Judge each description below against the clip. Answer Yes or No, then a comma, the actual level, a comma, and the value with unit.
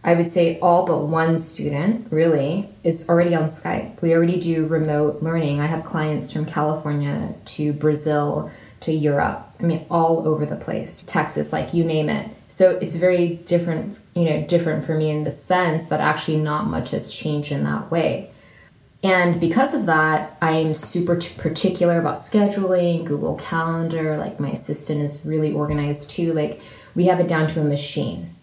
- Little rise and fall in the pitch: Yes, narrow, 2.2 semitones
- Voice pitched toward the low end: No, medium, 160 Hz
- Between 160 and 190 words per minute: Yes, average, 175 wpm